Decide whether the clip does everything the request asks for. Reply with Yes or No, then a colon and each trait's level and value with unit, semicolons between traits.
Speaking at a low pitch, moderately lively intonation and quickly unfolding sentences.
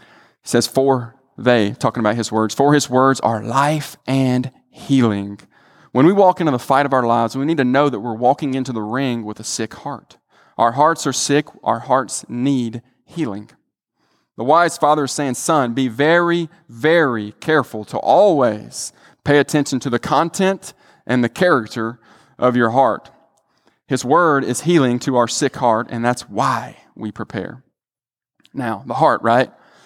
No: low, 130 Hz; average, 3.7 semitones; average, 170 wpm